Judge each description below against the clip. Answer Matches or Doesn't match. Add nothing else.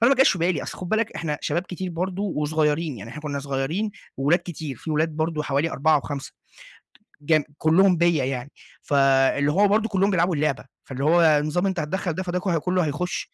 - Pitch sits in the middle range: Matches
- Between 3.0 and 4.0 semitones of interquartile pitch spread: Matches